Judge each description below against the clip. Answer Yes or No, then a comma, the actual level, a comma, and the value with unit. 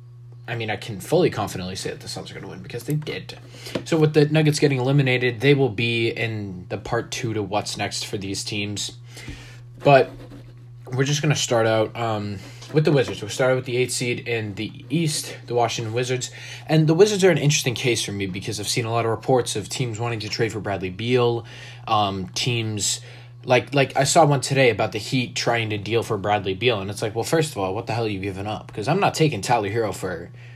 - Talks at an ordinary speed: No, fast, 240 wpm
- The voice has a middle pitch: No, low, 120 Hz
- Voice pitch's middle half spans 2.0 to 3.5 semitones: Yes, average, 2.9 semitones